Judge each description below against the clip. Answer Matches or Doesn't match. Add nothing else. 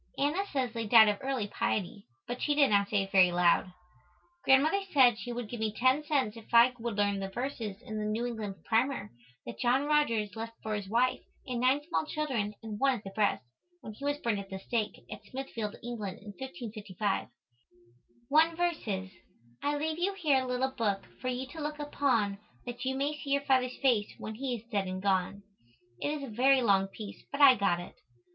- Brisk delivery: Matches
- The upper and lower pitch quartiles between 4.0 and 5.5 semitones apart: Matches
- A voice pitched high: Matches